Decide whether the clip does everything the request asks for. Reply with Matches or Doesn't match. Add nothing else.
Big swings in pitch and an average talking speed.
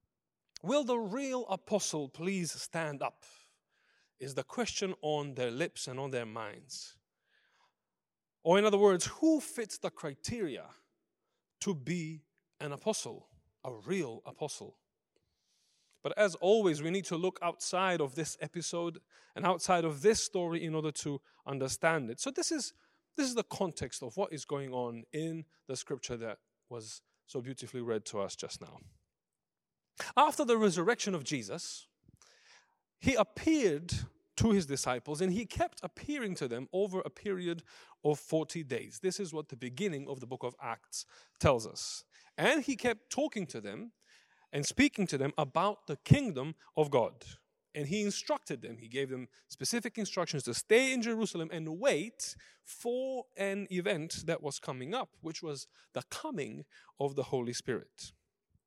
Matches